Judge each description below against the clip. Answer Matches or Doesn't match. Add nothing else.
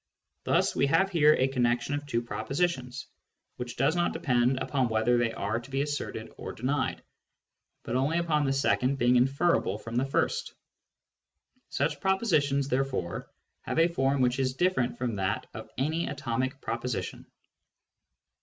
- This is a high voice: Doesn't match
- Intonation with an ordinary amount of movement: Matches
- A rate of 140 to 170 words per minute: Matches